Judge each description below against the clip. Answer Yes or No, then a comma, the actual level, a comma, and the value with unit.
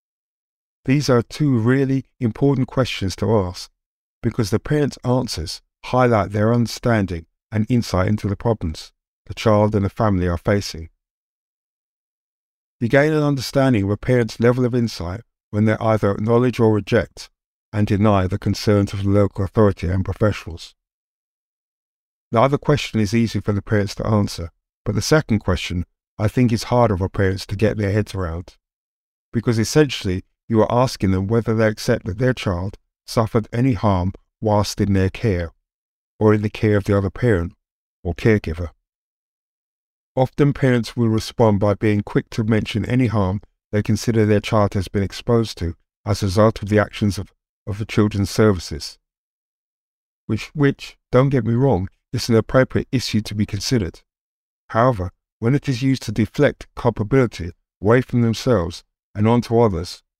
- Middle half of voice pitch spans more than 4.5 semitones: No, average, 3.2 semitones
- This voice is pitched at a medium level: No, low, 110 Hz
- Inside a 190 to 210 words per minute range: No, average, 165 wpm